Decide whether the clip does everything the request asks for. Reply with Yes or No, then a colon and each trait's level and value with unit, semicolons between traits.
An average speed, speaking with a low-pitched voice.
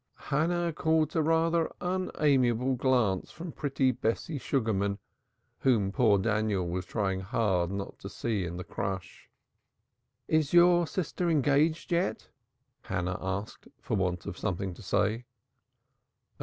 No: slow, 130 wpm; low, 120 Hz